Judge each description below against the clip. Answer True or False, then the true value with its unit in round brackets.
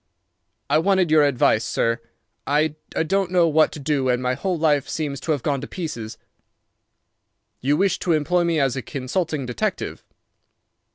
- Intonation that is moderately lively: True (3.9 semitones)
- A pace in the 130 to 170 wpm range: True (165 wpm)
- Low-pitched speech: False (150 Hz)